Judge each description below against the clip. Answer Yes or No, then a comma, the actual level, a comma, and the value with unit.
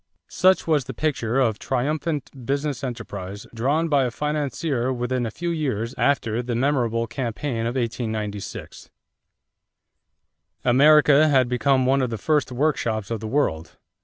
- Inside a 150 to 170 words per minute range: No, average, 140 wpm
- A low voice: Yes, low, 130 Hz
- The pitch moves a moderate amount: Yes, average, 3.9 semitones